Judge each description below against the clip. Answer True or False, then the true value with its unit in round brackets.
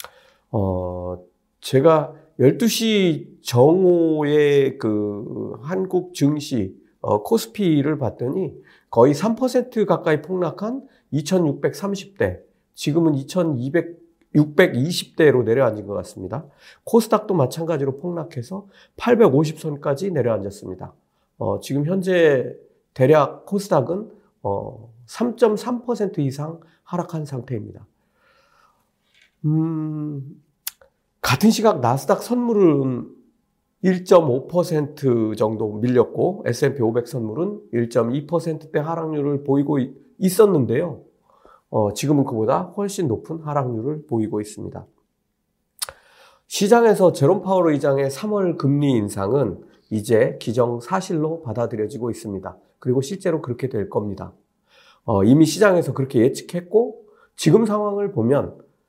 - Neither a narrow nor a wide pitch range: False (7.0 semitones)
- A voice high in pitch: False (155 Hz)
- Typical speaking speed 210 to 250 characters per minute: True (215 characters per minute)